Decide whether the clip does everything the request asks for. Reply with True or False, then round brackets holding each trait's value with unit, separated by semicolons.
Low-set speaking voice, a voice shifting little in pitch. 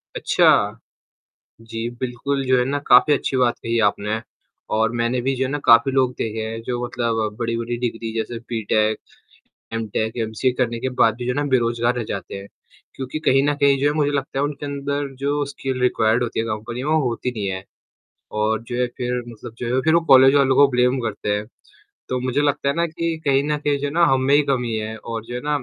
False (125 Hz; 3.3 semitones)